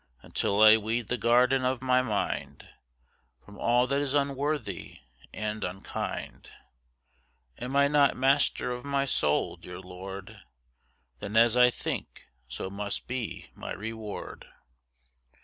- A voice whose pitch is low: Yes, low, 120 Hz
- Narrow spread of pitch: No, average, 4.3 semitones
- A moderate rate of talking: No, slow, 130 wpm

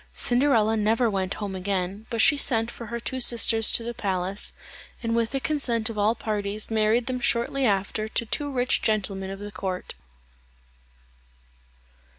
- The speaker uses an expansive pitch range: No, average, 2.8 semitones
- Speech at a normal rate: Yes, average, 160 wpm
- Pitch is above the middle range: Yes, high, 220 Hz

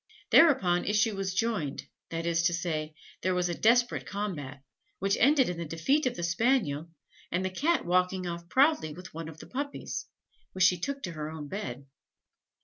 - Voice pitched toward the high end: No, medium, 180 Hz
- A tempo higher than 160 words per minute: Yes, average, 190 wpm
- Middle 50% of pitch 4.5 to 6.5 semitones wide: Yes, average, 5.3 semitones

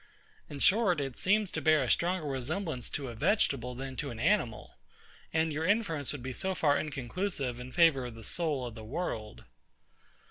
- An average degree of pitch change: No, wide, 5.8 semitones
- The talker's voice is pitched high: No, medium, 145 Hz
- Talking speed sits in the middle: Yes, average, 185 wpm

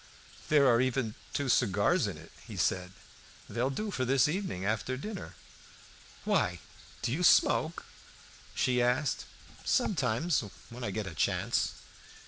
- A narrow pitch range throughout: No, average, 5.0 semitones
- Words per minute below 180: Yes, slow, 135 wpm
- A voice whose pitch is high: No, low, 130 Hz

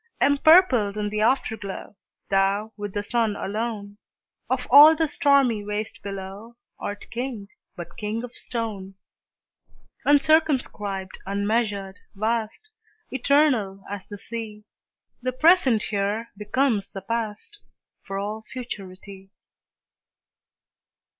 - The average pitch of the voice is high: Yes, high, 215 Hz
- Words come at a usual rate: No, slow, 105 wpm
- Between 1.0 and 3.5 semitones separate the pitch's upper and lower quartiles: No, average, 3.9 semitones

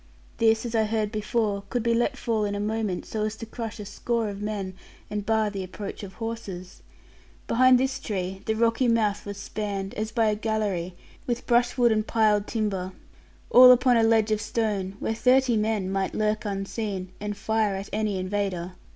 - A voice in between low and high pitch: No, high, 215 Hz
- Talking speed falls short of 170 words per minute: No, average, 190 wpm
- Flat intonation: Yes, narrow, 2.2 semitones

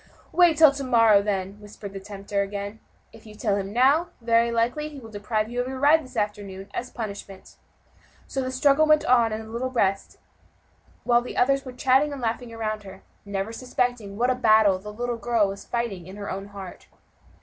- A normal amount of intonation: Yes, average, 4.0 semitones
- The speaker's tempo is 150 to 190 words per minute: No, fast, 205 wpm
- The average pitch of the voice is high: Yes, high, 225 Hz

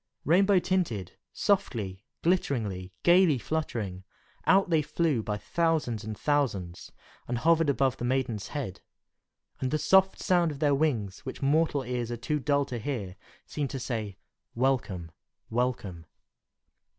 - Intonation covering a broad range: Yes, wide, 6.5 semitones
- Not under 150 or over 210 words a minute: No, average, 140 wpm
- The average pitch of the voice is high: No, low, 130 Hz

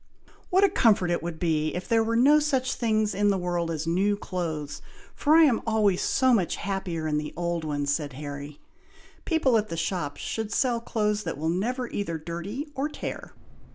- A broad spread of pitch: Yes, wide, 6.0 semitones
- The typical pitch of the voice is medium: No, high, 195 Hz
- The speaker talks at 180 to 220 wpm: Yes, average, 195 wpm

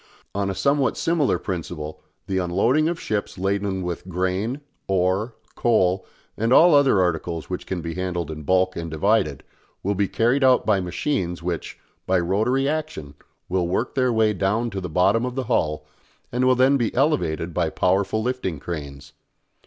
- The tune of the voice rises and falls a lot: Yes, wide, 5.7 semitones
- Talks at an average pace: Yes, average, 170 wpm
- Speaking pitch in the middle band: No, very low, 95 Hz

